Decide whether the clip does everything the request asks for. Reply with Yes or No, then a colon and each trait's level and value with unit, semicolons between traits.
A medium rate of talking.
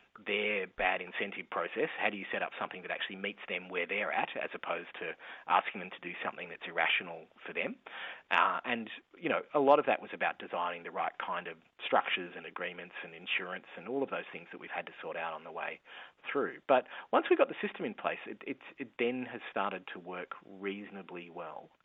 No: fast, 225 wpm